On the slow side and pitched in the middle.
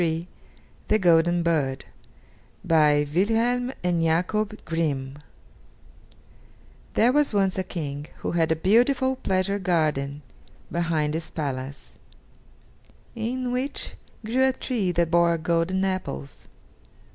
Yes: slow, 110 wpm; medium, 175 Hz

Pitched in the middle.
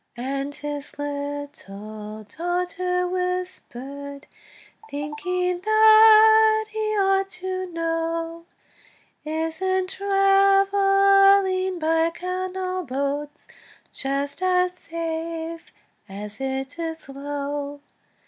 No: very high, 335 Hz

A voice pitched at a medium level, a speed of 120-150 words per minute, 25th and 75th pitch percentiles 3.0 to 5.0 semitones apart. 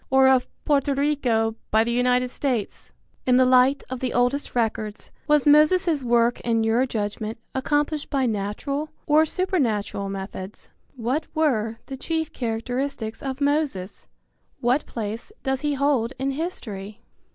No: very high, 255 Hz; average, 140 wpm; average, 4.3 semitones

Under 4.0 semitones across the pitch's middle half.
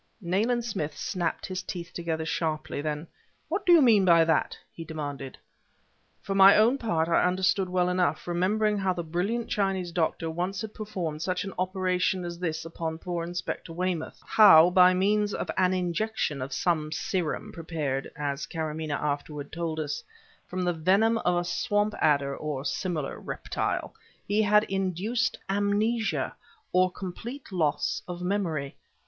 Yes: average, 3.5 semitones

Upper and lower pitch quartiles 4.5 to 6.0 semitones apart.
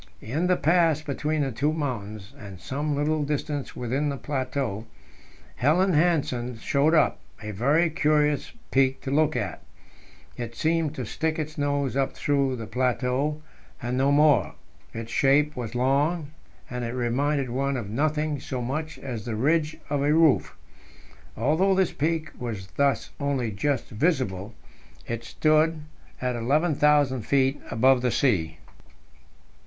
No: average, 3.7 semitones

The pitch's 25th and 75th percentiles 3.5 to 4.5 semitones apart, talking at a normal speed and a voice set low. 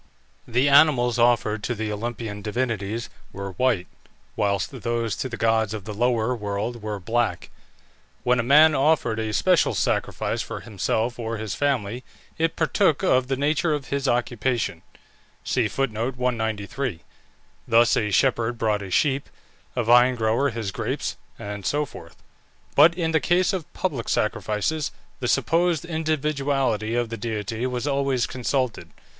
Yes: average, 4.1 semitones; average, 145 wpm; low, 120 Hz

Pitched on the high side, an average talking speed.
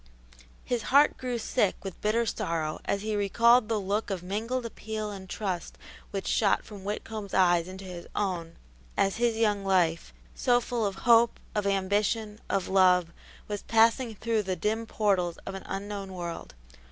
Yes: high, 205 Hz; average, 165 wpm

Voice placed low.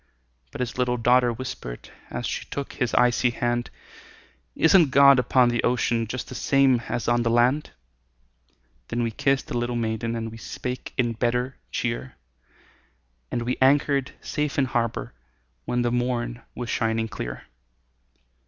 Yes: low, 120 Hz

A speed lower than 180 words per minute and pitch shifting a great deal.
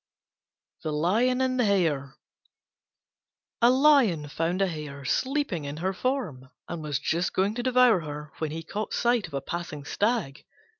Yes: average, 160 wpm; wide, 8.2 semitones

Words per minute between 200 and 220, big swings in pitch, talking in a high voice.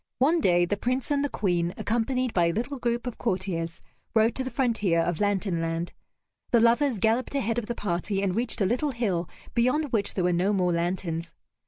Yes: fast, 205 wpm; wide, 5.7 semitones; high, 210 Hz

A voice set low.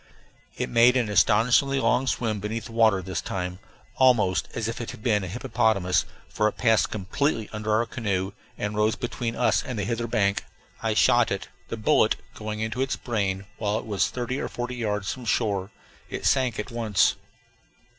Yes: low, 110 Hz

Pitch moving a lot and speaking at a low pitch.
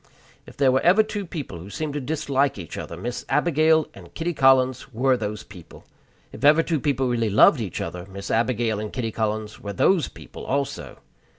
Yes: wide, 5.7 semitones; low, 130 Hz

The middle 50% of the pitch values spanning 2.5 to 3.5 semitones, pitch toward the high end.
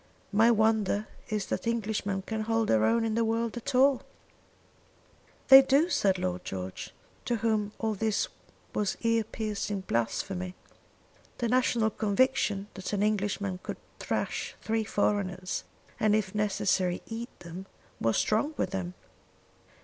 Yes: average, 2.9 semitones; high, 210 Hz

